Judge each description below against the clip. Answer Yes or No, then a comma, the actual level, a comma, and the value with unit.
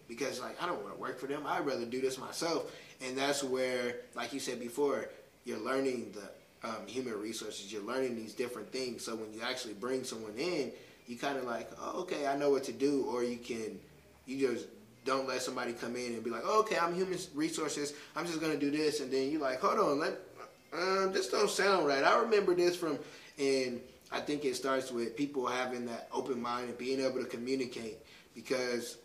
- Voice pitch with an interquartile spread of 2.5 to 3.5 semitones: Yes, average, 2.8 semitones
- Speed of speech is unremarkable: No, fast, 220 wpm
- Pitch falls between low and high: No, low, 130 Hz